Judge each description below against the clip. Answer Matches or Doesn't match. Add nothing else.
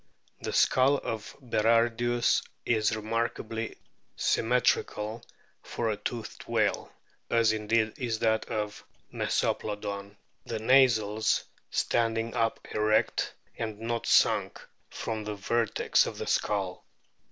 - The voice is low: Matches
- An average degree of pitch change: Doesn't match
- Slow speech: Matches